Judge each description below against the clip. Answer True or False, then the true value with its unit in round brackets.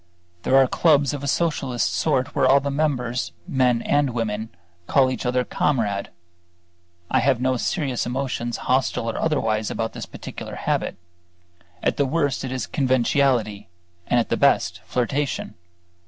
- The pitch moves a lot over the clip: False (2.8 semitones)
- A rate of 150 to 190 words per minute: True (155 wpm)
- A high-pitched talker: False (130 Hz)